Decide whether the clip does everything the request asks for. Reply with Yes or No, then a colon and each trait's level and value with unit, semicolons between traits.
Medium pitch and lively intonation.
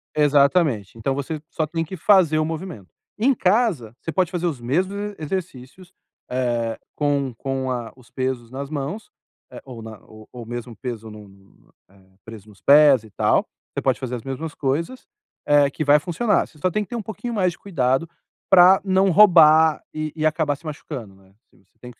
Yes: medium, 145 Hz; wide, 6.2 semitones